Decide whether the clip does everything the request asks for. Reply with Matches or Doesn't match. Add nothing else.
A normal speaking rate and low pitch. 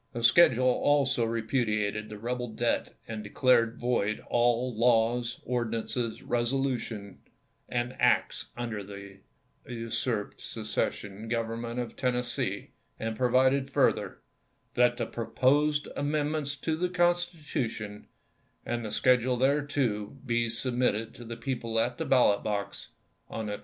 Doesn't match